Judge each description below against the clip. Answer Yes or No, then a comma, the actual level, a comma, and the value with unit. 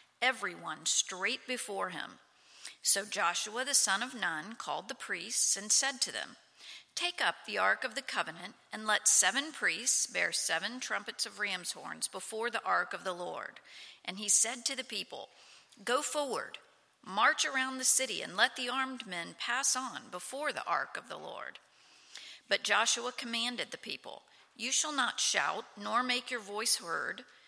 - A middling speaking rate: Yes, average, 175 wpm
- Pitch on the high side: Yes, high, 240 Hz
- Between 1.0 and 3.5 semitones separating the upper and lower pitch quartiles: No, average, 4.0 semitones